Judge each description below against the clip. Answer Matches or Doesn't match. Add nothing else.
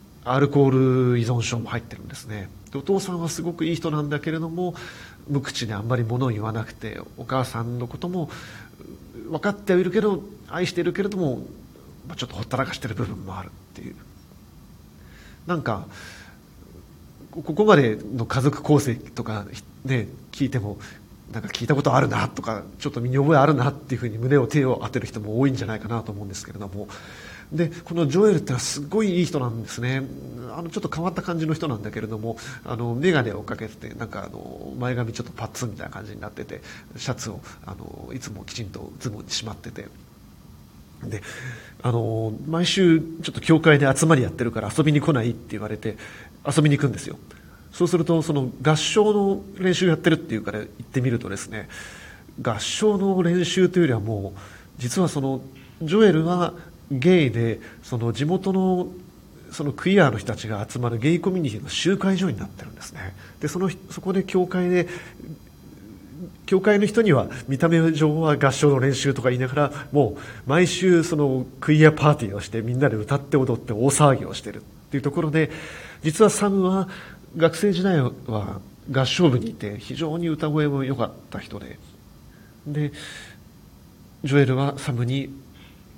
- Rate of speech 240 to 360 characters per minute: Doesn't match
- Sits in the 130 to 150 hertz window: Matches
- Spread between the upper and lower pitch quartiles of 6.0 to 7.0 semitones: Matches